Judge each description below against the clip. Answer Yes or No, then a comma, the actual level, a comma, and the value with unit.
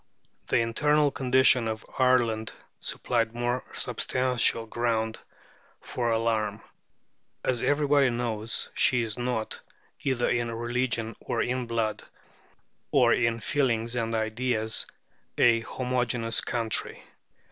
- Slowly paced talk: Yes, slow, 105 wpm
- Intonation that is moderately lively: No, narrow, 1.9 semitones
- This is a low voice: Yes, low, 120 Hz